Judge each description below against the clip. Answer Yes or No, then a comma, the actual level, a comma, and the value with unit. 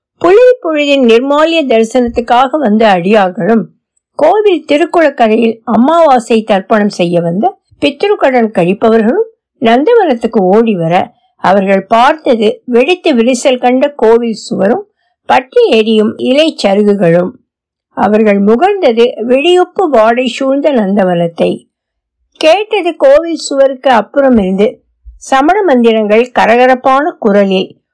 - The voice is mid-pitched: No, high, 245 Hz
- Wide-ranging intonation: Yes, wide, 6.0 semitones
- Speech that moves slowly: No, average, 85 wpm